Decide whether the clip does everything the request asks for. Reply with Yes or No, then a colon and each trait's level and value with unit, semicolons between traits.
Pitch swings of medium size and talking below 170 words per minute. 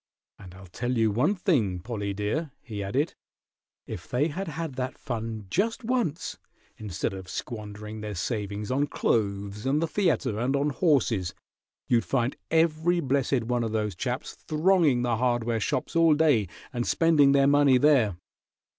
No: wide, 6.1 semitones; average, 160 wpm